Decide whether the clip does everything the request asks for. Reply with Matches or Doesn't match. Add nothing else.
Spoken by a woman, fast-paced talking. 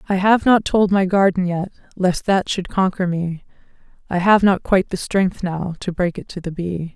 Matches